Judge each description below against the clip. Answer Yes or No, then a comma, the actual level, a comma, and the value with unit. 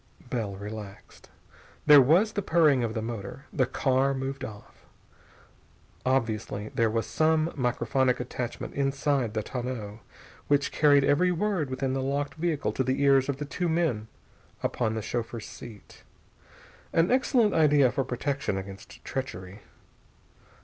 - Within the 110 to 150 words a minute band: Yes, average, 140 wpm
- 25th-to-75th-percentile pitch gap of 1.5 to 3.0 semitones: No, average, 4.2 semitones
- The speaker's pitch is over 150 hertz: No, low, 130 Hz